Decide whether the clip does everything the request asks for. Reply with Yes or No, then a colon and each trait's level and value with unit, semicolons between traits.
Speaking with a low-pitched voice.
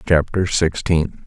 Yes: very low, 85 Hz